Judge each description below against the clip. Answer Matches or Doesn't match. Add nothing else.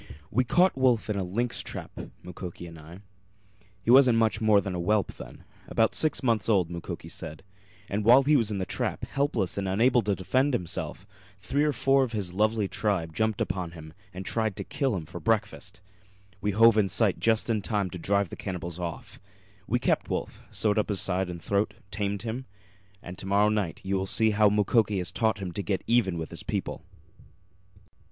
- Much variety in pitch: Doesn't match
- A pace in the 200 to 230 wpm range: Matches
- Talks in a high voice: Doesn't match